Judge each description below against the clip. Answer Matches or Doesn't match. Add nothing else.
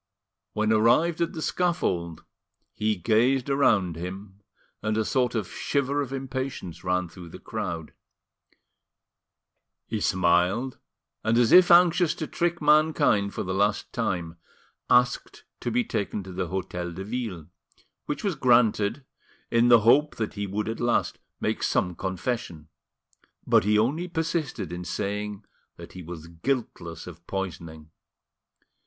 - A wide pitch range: Matches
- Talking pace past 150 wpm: Doesn't match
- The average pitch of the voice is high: Doesn't match